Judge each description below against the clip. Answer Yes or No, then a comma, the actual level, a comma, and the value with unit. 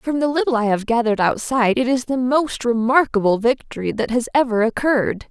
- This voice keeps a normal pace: Yes, average, 190 wpm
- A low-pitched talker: No, high, 245 Hz